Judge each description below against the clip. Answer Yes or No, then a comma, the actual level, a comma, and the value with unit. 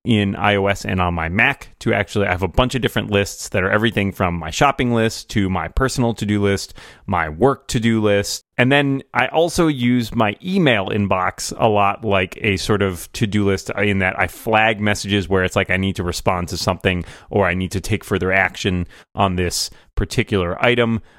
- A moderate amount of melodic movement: Yes, average, 3.6 semitones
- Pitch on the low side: Yes, low, 100 Hz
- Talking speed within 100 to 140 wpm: No, fast, 205 wpm